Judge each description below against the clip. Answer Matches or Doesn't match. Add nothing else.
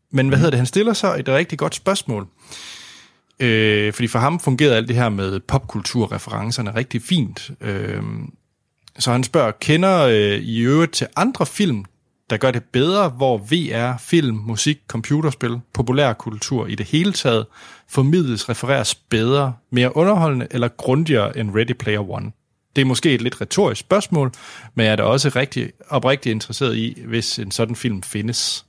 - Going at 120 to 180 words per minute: Matches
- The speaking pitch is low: Matches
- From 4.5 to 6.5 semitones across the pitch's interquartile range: Doesn't match